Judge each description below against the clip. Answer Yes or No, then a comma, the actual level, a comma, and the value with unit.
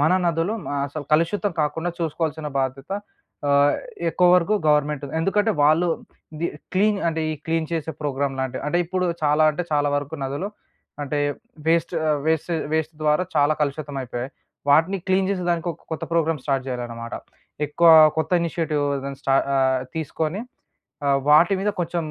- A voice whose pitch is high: No, medium, 155 Hz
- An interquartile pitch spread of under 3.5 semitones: Yes, average, 3.0 semitones